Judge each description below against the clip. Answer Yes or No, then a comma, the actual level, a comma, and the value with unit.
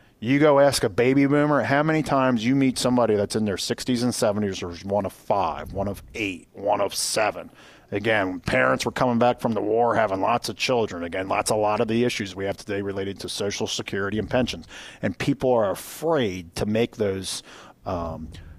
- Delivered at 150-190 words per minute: No, fast, 205 wpm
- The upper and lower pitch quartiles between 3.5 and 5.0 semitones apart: Yes, average, 4.6 semitones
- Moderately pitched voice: No, low, 110 Hz